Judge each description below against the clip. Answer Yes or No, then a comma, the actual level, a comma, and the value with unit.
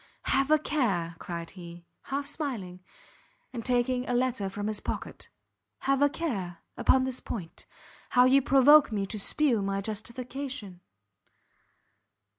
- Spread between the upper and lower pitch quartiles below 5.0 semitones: No, wide, 5.6 semitones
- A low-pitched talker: No, high, 245 Hz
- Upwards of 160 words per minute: No, slow, 135 wpm